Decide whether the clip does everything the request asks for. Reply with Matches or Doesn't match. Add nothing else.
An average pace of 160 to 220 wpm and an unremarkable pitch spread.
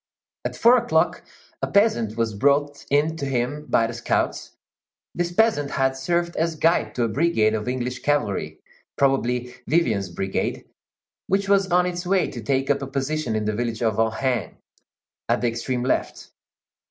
Doesn't match